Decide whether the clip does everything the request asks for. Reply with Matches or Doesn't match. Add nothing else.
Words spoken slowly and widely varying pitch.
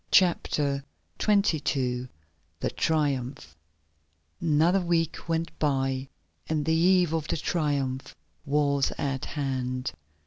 Doesn't match